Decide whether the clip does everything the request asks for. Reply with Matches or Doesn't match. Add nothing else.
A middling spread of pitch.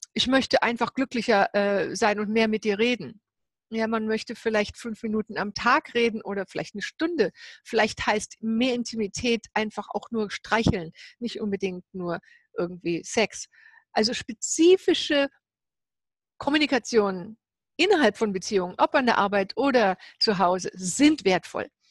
Matches